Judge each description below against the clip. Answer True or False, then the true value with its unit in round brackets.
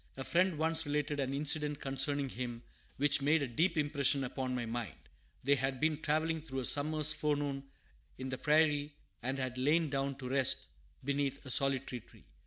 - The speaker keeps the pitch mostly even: True (2.2 semitones)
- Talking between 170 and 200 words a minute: True (180 wpm)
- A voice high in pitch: False (140 Hz)